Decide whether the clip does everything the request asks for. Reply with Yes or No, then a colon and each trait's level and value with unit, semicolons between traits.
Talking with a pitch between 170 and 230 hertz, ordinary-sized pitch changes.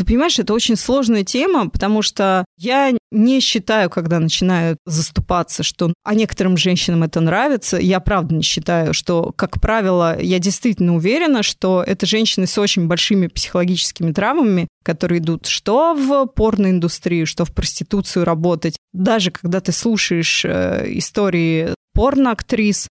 Yes: medium, 185 Hz; average, 4.3 semitones